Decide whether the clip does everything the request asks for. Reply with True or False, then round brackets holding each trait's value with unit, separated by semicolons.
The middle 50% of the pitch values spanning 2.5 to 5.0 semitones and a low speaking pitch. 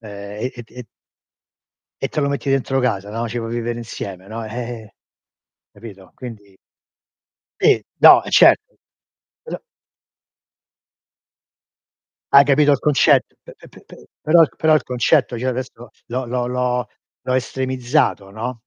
True (2.8 semitones; 125 Hz)